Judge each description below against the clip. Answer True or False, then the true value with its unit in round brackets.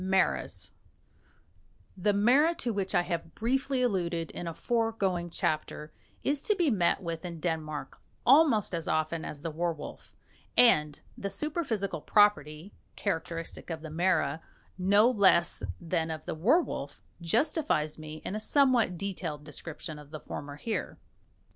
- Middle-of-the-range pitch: True (175 Hz)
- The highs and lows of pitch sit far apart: True (5.9 semitones)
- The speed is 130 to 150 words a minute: True (140 wpm)